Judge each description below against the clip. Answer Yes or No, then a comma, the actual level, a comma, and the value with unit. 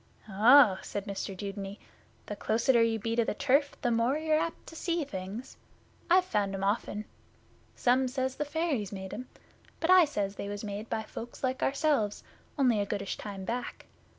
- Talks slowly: No, average, 180 wpm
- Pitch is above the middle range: Yes, high, 230 Hz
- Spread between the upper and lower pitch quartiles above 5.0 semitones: Yes, wide, 5.4 semitones